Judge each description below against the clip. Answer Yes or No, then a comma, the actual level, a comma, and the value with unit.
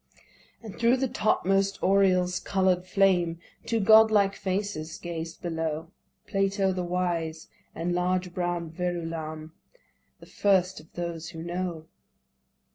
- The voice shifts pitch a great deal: No, average, 2.8 semitones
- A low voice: No, medium, 180 Hz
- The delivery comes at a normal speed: No, slow, 120 wpm